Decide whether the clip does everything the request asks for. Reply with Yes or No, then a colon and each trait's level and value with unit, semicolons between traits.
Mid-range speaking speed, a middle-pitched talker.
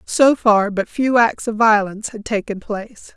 No: average, 190 wpm; high, 215 Hz